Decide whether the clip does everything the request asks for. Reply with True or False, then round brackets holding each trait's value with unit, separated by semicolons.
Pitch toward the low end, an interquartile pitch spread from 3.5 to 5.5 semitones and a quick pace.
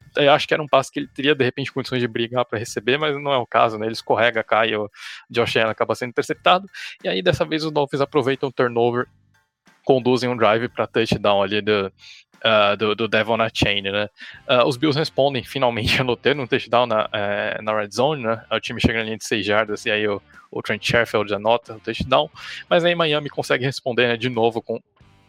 True (120 Hz; 4.2 semitones; 220 wpm)